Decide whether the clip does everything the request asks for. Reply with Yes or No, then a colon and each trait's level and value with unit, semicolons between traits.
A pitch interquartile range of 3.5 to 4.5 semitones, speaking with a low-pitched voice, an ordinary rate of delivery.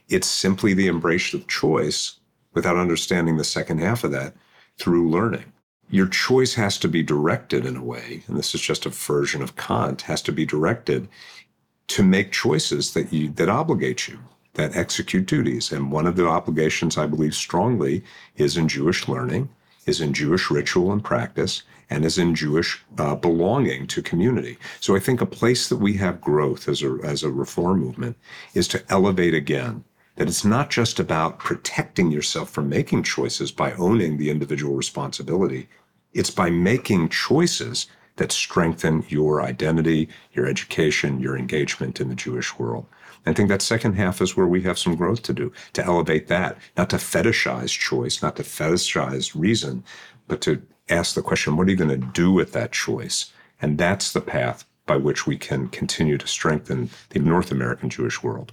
Yes: average, 4.2 semitones; very low, 80 Hz; average, 180 wpm